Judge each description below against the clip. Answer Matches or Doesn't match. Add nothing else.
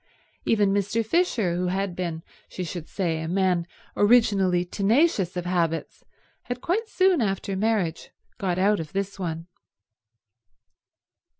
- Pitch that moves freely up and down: Doesn't match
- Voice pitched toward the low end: Doesn't match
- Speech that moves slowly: Matches